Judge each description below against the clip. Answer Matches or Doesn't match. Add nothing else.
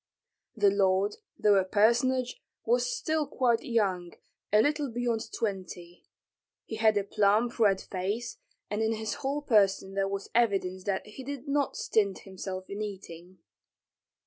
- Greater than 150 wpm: Doesn't match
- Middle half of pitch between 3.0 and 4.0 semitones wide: Matches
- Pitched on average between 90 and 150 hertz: Doesn't match